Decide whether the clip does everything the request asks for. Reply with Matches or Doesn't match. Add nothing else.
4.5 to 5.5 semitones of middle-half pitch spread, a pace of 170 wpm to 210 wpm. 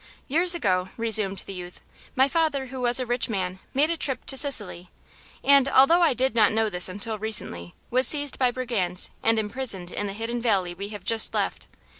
Matches